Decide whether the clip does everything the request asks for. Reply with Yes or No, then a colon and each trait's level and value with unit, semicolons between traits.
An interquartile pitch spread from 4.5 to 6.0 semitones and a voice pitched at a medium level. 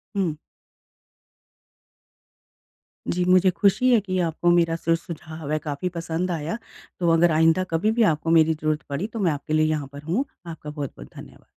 No: average, 2.8 semitones; medium, 165 Hz